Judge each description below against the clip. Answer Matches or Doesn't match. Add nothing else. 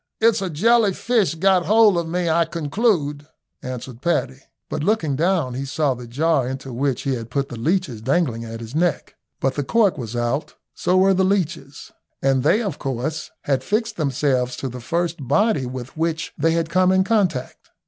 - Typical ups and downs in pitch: Doesn't match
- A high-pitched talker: Doesn't match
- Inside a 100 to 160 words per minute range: Doesn't match